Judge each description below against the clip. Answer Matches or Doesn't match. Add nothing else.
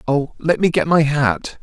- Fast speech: Doesn't match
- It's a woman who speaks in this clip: Doesn't match